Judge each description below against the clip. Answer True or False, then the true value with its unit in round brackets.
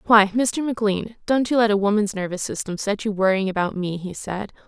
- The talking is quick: True (220 wpm)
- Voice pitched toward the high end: True (205 Hz)